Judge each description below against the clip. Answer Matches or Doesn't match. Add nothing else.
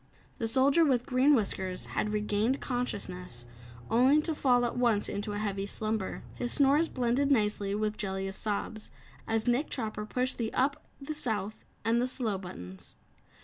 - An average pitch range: Matches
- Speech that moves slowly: Doesn't match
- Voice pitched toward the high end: Matches